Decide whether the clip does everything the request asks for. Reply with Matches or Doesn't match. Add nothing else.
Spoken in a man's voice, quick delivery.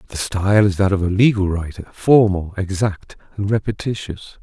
Doesn't match